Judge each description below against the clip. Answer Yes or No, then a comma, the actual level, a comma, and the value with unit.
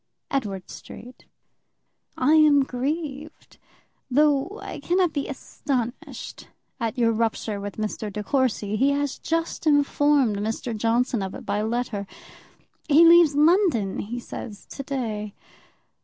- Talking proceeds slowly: Yes, slow, 130 wpm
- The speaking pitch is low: No, very high, 255 Hz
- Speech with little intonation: No, average, 5.3 semitones